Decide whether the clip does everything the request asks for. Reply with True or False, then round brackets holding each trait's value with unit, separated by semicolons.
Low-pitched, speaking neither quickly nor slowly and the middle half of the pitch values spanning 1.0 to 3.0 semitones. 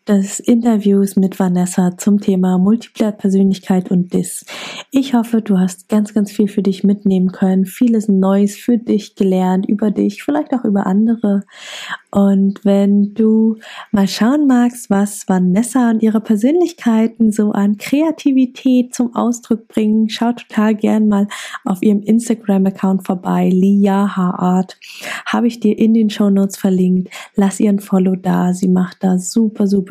False (205 Hz; 145 wpm; 2.7 semitones)